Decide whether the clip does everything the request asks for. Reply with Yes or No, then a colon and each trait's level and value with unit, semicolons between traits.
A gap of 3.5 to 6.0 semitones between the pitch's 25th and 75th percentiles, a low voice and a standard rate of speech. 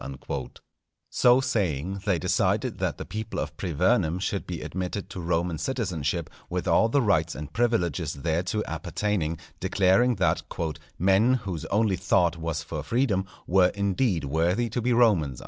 Yes: average, 4.6 semitones; very low, 95 Hz; average, 150 wpm